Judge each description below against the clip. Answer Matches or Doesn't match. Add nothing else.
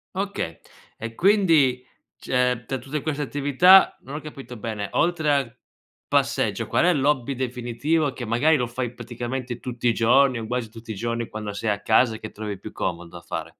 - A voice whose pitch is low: Matches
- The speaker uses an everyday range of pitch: Matches